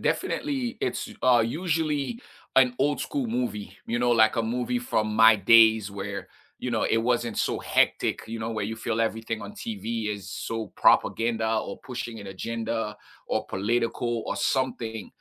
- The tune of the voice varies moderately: No, narrow, 2.2 semitones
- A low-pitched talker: Yes, low, 115 Hz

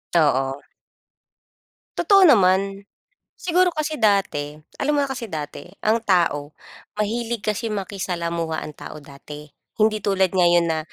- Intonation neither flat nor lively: No, wide, 6.3 semitones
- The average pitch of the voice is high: Yes, high, 195 Hz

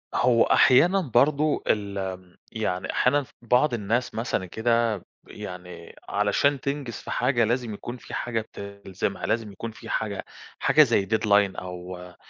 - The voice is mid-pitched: No, low, 110 Hz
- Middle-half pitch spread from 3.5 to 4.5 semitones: Yes, average, 3.9 semitones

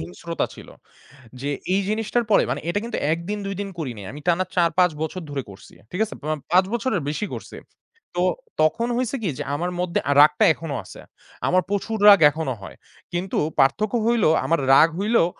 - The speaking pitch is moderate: Yes, medium, 180 Hz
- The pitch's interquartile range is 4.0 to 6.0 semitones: Yes, average, 5.1 semitones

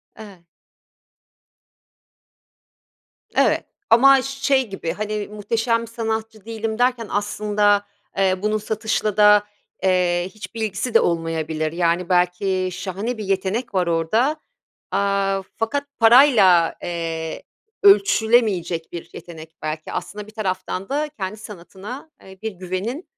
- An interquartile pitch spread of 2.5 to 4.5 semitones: Yes, average, 3.7 semitones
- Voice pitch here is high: Yes, high, 205 Hz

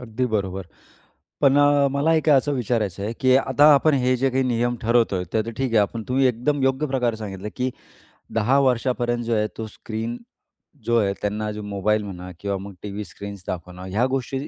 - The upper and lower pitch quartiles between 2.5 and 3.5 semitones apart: No, average, 4.2 semitones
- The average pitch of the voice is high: No, low, 120 Hz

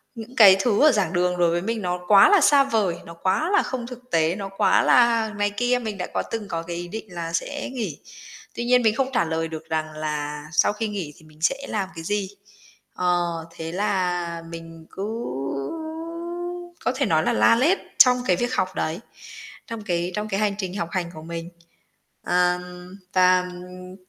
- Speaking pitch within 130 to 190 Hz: Yes, medium, 185 Hz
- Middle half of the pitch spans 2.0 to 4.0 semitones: No, average, 4.9 semitones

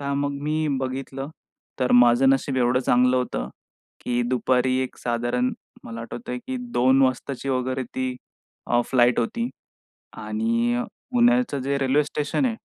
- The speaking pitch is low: Yes, low, 130 Hz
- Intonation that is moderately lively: Yes, average, 3.3 semitones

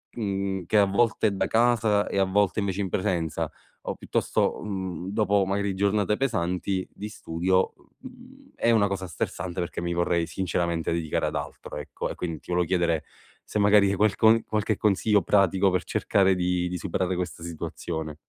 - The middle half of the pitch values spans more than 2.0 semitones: Yes, average, 2.8 semitones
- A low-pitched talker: Yes, very low, 95 Hz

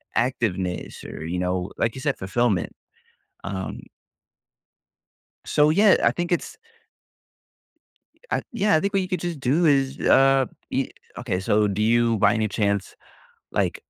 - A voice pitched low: Yes, low, 120 Hz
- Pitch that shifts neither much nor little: No, wide, 7.4 semitones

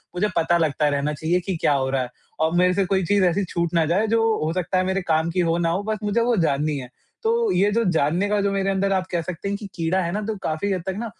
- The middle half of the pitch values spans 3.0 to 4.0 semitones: Yes, average, 3.7 semitones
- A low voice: No, medium, 180 Hz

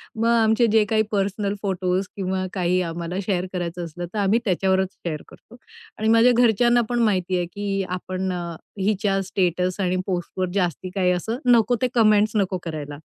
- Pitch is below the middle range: No, high, 190 Hz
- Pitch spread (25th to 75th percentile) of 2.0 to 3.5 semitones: Yes, average, 3.1 semitones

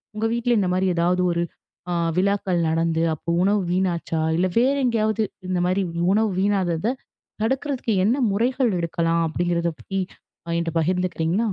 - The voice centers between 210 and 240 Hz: No, medium, 185 Hz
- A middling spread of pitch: Yes, average, 4.1 semitones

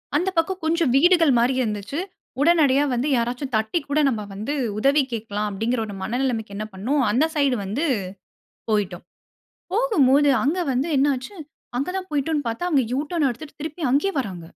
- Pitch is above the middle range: Yes, very high, 270 Hz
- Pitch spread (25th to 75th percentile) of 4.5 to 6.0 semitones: Yes, wide, 5.5 semitones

